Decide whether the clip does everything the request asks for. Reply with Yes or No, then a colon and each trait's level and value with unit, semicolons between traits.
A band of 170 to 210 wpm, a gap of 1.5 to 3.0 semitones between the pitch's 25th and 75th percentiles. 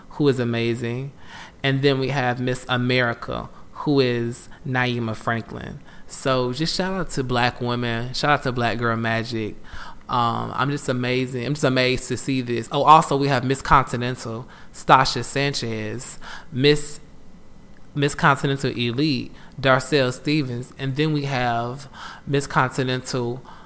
No: average, 140 wpm; average, 2.7 semitones